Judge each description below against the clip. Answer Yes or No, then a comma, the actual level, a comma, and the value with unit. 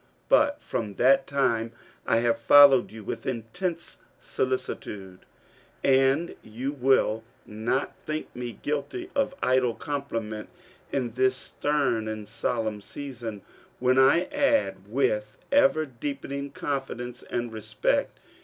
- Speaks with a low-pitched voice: Yes, low, 130 Hz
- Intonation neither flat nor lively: Yes, average, 3.9 semitones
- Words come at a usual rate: No, slow, 120 wpm